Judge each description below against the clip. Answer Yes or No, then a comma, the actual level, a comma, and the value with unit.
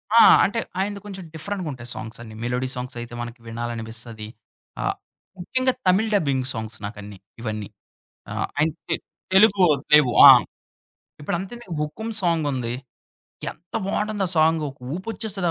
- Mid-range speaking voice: Yes, medium, 150 Hz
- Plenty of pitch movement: Yes, wide, 8.5 semitones